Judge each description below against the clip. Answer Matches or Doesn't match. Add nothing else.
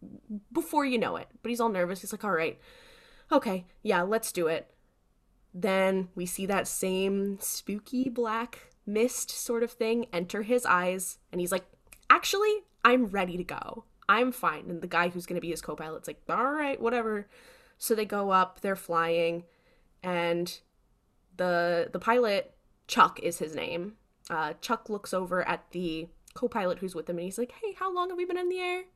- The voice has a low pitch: Doesn't match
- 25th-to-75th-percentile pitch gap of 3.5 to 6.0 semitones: Matches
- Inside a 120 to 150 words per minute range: Doesn't match